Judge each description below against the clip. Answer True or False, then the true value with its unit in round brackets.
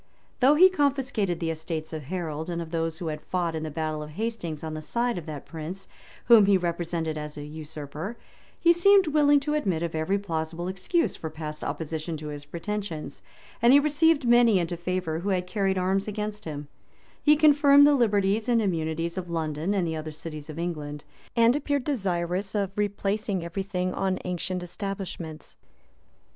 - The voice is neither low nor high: True (180 Hz)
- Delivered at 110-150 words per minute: False (185 wpm)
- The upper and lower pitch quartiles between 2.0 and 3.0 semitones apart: False (5.1 semitones)